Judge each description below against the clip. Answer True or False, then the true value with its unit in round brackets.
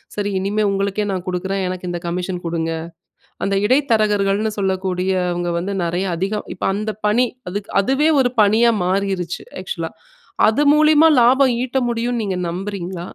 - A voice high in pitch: True (200 Hz)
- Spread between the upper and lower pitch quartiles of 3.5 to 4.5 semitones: True (3.8 semitones)